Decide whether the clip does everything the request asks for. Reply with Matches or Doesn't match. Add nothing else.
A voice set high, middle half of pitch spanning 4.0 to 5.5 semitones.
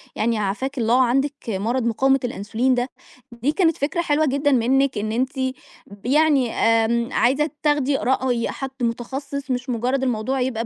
Doesn't match